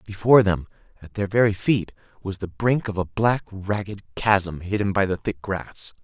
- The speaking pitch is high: No, low, 100 Hz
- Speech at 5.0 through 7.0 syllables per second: No, 4.6 syllables/s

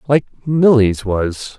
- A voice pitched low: Yes, low, 120 Hz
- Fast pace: No, slow, 115 wpm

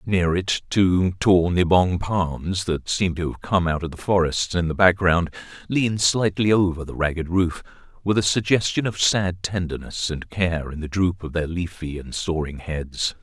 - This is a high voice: No, very low, 90 Hz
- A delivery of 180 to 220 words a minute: Yes, average, 185 wpm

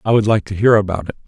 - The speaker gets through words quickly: Yes, fast, 330 wpm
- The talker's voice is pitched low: Yes, low, 105 Hz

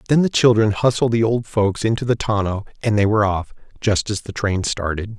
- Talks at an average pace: No, fast, 220 wpm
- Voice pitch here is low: Yes, low, 105 Hz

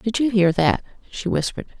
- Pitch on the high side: Yes, high, 200 Hz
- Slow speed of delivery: No, average, 200 wpm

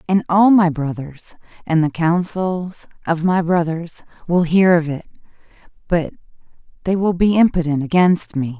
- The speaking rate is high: No, average, 145 wpm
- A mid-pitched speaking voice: Yes, medium, 170 Hz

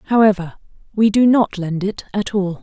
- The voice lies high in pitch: Yes, high, 200 Hz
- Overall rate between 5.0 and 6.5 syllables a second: No, 4.6 syllables/s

